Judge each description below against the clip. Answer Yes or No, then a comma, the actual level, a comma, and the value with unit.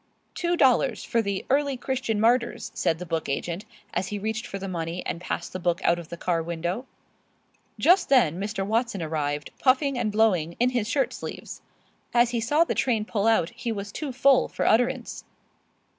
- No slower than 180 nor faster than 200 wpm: Yes, average, 190 wpm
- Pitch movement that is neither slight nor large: No, wide, 6.0 semitones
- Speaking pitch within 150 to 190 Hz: No, high, 220 Hz